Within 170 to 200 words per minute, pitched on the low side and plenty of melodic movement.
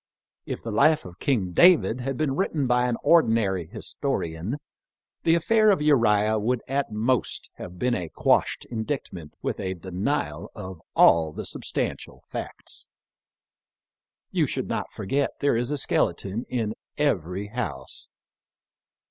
No: average, 140 wpm; low, 115 Hz; wide, 6.7 semitones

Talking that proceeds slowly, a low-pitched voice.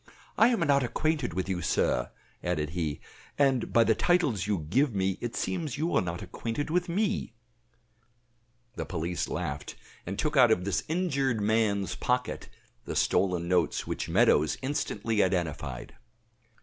No: average, 150 wpm; low, 110 Hz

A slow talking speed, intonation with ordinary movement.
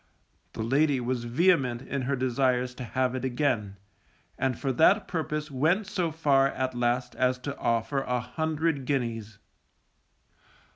No: average, 145 wpm; average, 3.2 semitones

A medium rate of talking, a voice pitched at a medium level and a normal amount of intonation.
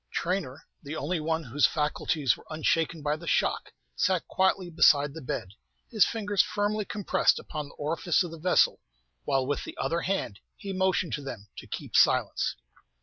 Yes: average, 175 wpm; medium, 165 Hz; average, 4.3 semitones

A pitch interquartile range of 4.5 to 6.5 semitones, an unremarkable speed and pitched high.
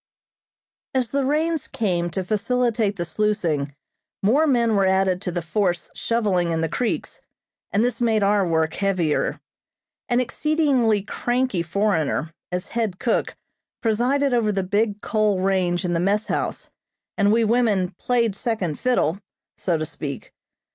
Yes: average, 4.8 semitones; average, 150 wpm; high, 205 Hz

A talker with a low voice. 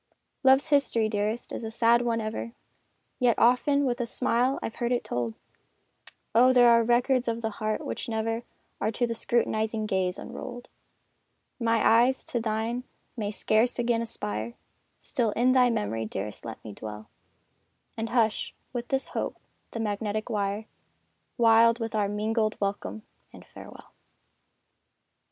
No: high, 225 Hz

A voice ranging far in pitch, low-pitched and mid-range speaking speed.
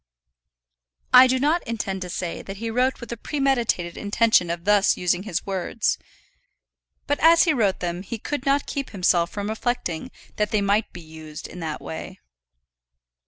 No: wide, 5.7 semitones; high, 205 Hz; average, 170 wpm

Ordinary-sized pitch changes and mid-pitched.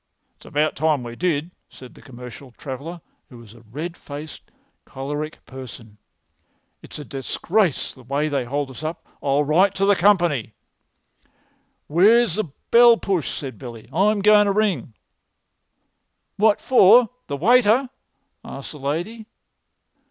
No: wide, 7.0 semitones; medium, 155 Hz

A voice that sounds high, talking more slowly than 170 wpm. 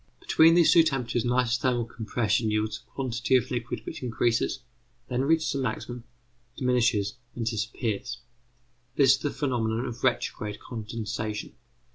No: low, 120 Hz; average, 140 wpm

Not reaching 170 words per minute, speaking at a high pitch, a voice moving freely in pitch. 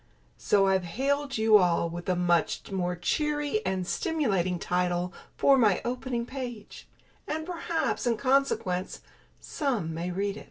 Yes: average, 145 wpm; high, 210 Hz; wide, 7.3 semitones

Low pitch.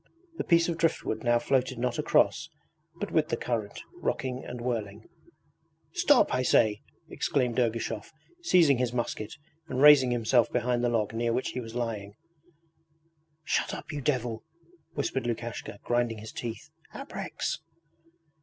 Yes: low, 120 Hz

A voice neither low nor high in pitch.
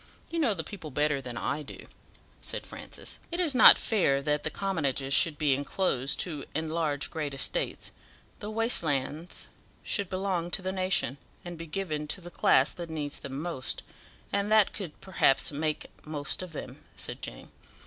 Yes: medium, 160 Hz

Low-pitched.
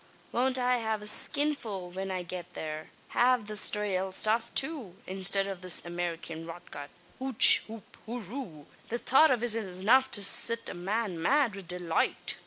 No: high, 205 Hz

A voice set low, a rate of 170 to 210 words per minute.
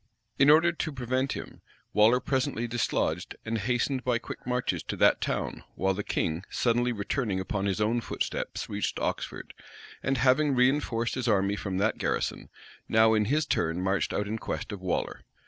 Yes: low, 115 Hz; average, 175 wpm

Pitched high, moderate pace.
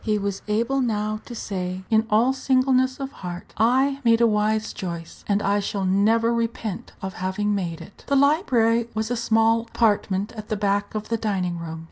Yes: high, 215 Hz; average, 190 wpm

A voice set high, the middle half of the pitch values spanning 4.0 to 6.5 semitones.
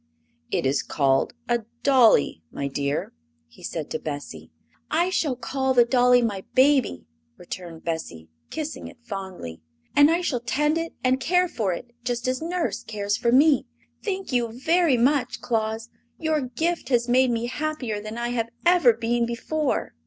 Yes: high, 245 Hz; average, 5.1 semitones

